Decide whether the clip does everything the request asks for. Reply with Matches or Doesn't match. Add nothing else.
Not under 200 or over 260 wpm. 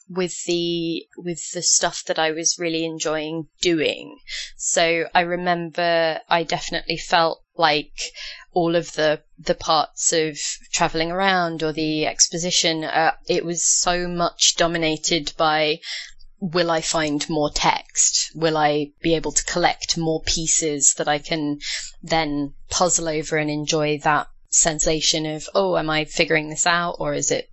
Doesn't match